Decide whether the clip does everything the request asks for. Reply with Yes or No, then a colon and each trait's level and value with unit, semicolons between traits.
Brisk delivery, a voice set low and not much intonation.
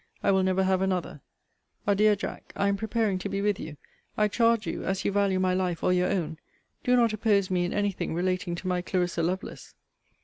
No: fast, 215 wpm; high, 190 Hz; narrow, 2.0 semitones